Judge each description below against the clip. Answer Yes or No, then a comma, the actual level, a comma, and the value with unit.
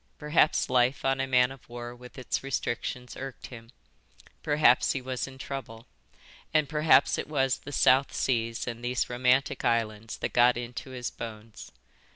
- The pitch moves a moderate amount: No, narrow, 2.0 semitones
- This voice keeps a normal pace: Yes, average, 165 wpm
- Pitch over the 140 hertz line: No, low, 125 Hz